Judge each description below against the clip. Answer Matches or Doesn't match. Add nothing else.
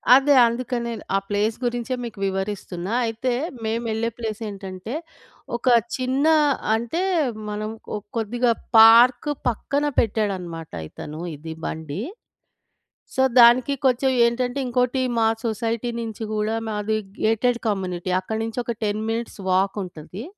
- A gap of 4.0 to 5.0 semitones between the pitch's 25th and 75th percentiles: Doesn't match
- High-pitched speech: Matches